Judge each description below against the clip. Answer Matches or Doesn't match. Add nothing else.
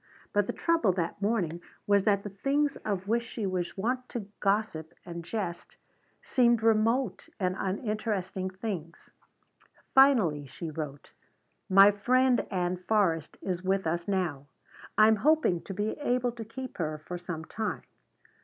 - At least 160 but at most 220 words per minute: Doesn't match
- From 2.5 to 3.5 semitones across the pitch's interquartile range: Doesn't match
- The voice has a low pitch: Doesn't match